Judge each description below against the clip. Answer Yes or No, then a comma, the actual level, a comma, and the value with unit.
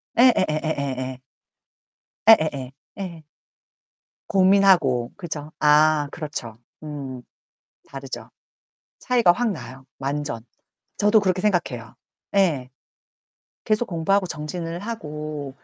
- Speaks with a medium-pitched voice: Yes, medium, 155 Hz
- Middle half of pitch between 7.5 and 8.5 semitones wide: No, wide, 5.8 semitones